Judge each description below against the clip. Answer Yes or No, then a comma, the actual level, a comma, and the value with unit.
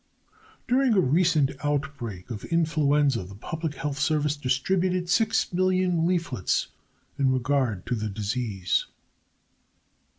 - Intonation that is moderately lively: No, wide, 6.0 semitones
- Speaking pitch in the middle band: Yes, medium, 145 Hz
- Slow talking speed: Yes, slow, 105 wpm